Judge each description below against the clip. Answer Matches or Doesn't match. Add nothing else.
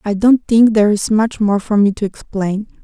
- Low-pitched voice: Doesn't match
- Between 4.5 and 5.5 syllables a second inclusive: Matches